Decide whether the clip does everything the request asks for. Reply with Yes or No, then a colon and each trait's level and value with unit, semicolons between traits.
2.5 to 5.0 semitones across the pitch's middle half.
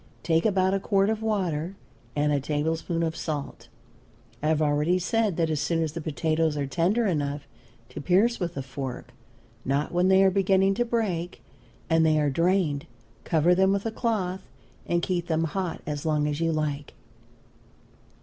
Yes: average, 4.1 semitones